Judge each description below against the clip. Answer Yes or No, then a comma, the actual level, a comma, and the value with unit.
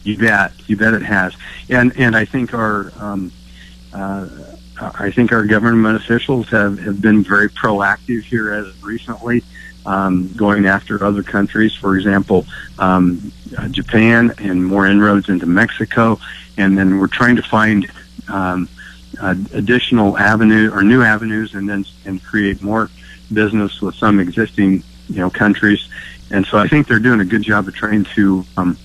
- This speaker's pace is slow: No, average, 165 wpm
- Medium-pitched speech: No, low, 105 Hz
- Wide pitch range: No, narrow, 2.4 semitones